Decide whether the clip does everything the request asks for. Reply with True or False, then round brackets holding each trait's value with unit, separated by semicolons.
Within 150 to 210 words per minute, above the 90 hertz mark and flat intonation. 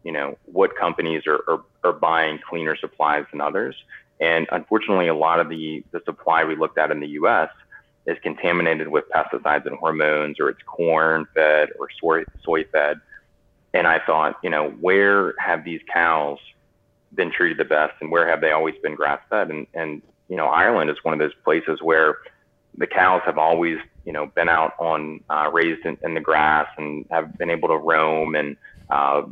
False (195 wpm; 80 Hz; 1.5 semitones)